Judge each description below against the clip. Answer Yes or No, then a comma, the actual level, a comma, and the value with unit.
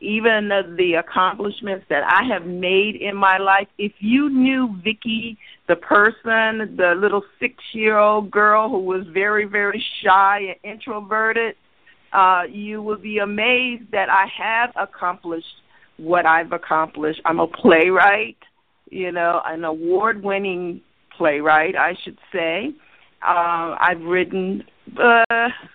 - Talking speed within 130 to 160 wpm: Yes, slow, 135 wpm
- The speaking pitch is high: Yes, high, 200 Hz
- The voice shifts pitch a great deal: No, average, 3.4 semitones